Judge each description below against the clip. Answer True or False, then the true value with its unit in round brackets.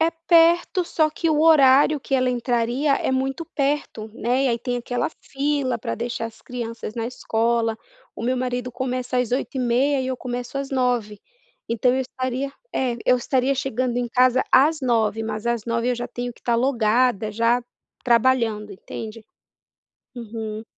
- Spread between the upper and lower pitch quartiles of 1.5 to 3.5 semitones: True (2.4 semitones)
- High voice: True (250 Hz)